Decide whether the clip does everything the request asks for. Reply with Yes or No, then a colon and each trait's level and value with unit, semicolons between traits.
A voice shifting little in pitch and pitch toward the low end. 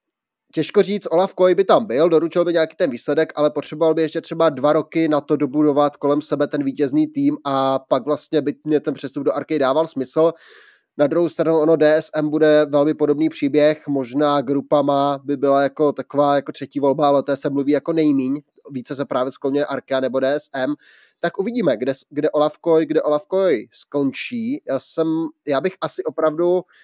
No: narrow, 2.1 semitones; medium, 150 Hz